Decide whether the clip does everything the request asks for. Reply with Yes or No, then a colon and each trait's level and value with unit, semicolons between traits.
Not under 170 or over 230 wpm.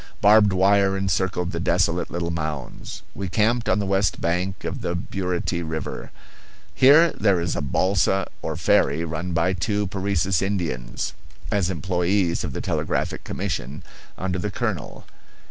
No: average, 145 wpm